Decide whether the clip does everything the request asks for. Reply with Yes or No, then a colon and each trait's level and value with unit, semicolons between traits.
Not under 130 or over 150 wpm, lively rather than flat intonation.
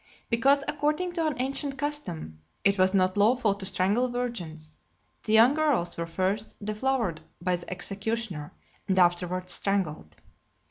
Yes: average, 140 wpm; wide, 6.1 semitones